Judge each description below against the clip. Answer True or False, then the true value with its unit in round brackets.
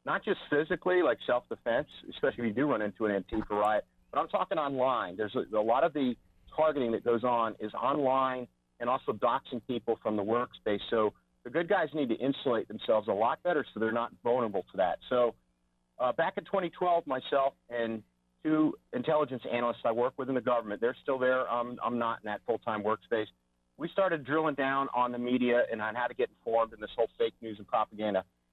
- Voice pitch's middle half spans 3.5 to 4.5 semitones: True (4.1 semitones)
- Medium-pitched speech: False (120 Hz)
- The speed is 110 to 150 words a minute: False (205 wpm)